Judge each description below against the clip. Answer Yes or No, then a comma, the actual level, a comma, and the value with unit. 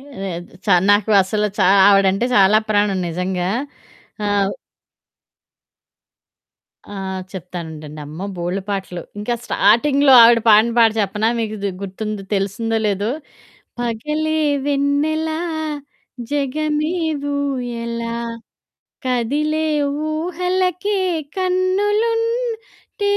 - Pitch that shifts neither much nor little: No, wide, 7.6 semitones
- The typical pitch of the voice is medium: No, high, 230 Hz